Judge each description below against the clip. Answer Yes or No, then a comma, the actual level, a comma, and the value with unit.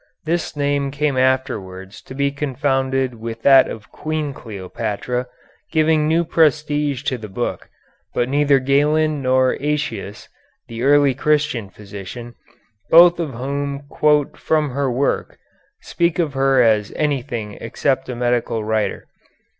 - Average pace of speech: No, slow, 130 wpm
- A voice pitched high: No, low, 135 Hz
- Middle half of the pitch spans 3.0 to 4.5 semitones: Yes, average, 3.7 semitones